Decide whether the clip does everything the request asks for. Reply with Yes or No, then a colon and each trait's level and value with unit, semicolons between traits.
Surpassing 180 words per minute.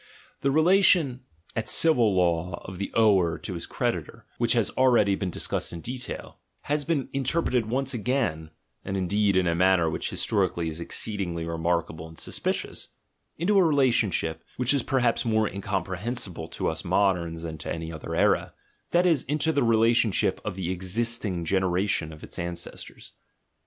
No: average, 160 wpm